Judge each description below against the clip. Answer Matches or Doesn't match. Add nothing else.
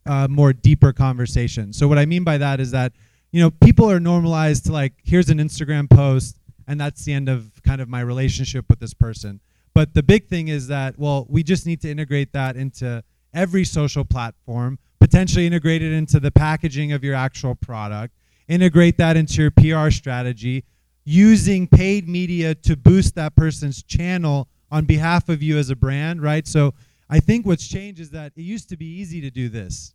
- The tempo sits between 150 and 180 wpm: Doesn't match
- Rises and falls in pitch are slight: Doesn't match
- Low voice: Doesn't match